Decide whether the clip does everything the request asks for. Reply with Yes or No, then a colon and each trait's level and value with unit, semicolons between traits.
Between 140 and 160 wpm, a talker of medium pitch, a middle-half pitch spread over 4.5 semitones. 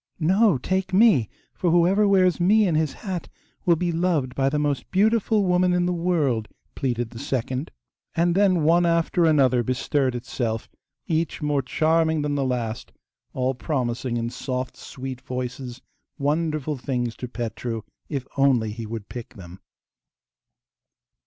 Yes: average, 150 wpm; medium, 145 Hz; wide, 5.6 semitones